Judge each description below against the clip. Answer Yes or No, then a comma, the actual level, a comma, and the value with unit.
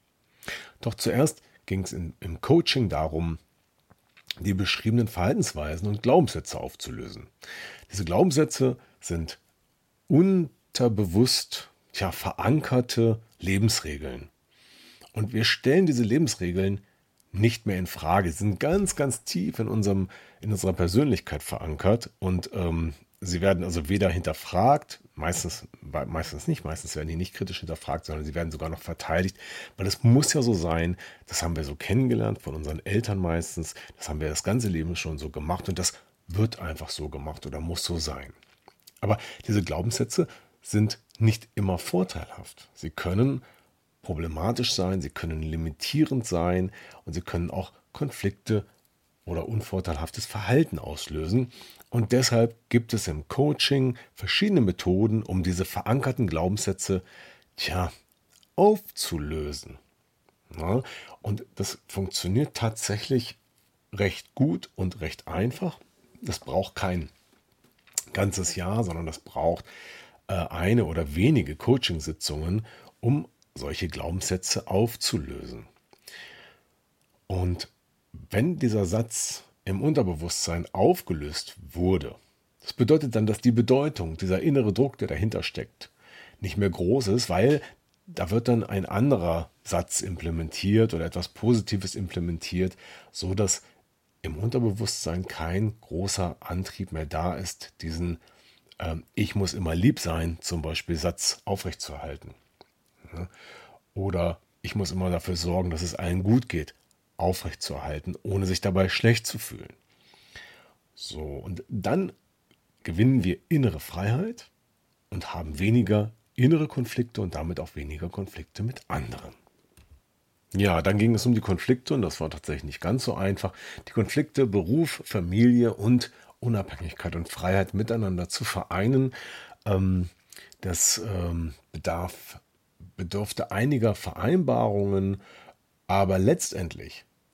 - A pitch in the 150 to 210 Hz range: No, very low, 95 Hz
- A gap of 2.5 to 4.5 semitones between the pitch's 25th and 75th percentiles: No, average, 5.3 semitones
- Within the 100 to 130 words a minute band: Yes, slow, 125 wpm